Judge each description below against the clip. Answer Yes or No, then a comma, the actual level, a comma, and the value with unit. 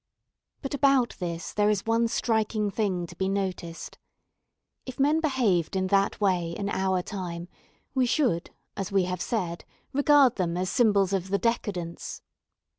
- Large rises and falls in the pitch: No, average, 4.5 semitones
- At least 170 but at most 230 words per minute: No, average, 155 wpm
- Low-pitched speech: No, high, 200 Hz